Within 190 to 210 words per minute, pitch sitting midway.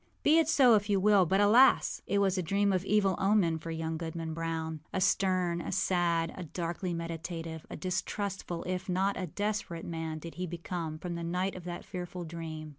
Yes: average, 200 wpm; medium, 175 Hz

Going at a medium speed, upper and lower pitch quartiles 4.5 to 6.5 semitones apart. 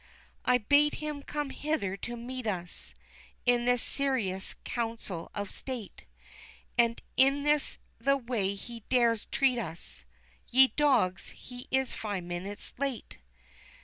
No: slow, 130 wpm; average, 4.9 semitones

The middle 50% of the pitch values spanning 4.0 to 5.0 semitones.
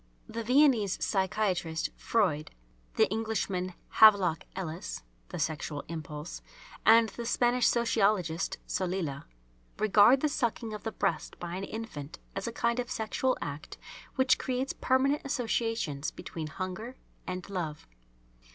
No: wide, 5.5 semitones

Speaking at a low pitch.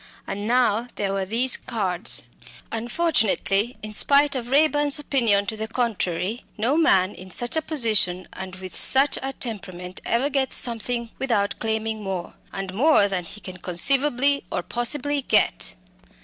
No: high, 225 Hz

